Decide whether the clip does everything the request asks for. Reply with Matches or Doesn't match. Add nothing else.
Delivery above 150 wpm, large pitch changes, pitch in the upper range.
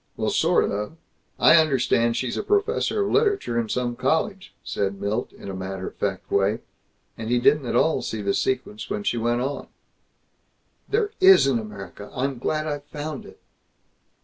Doesn't match